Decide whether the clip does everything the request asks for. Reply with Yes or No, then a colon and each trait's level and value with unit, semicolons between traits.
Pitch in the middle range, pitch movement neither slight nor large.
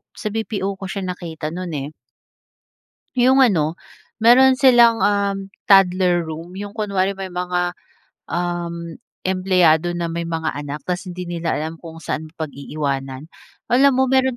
Yes: medium, 180 Hz; average, 3.7 semitones